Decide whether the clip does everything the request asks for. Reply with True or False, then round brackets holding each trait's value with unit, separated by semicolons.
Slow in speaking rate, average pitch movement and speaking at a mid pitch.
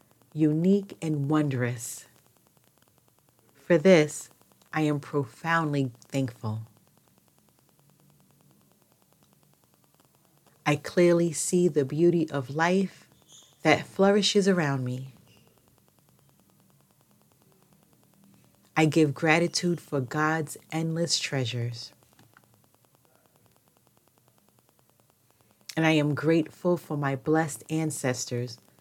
True (75 wpm; 3.6 semitones; 150 Hz)